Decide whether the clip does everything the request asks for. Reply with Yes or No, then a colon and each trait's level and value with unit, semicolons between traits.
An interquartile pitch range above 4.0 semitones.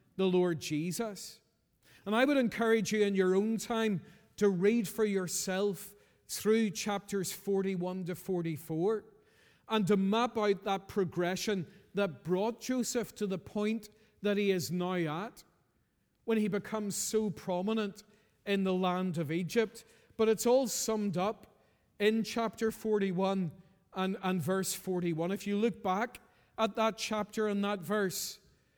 No: average, 3.0 semitones